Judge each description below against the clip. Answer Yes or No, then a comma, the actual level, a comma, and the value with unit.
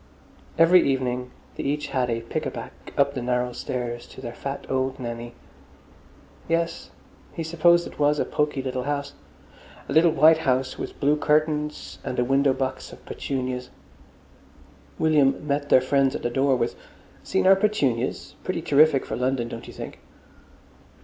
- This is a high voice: No, low, 135 Hz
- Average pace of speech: Yes, average, 165 wpm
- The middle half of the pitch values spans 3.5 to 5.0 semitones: No, average, 3.1 semitones